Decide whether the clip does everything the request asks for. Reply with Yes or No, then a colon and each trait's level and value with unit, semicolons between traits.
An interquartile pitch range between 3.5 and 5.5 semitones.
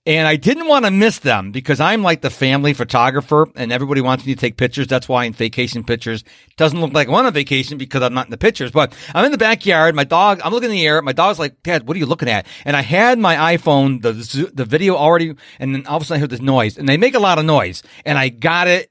Yes: average, 4.5 semitones